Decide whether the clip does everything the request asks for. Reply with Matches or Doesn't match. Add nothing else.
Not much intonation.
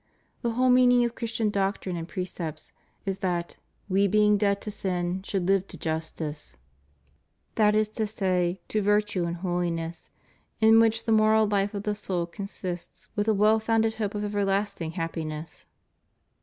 Doesn't match